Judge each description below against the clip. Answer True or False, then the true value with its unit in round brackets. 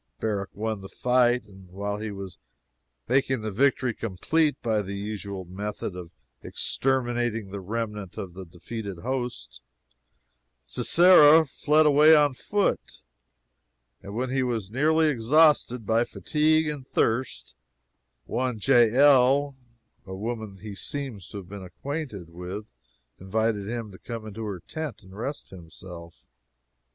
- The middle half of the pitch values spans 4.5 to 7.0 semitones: True (5.2 semitones)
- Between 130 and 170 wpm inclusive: True (135 wpm)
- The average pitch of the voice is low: True (110 Hz)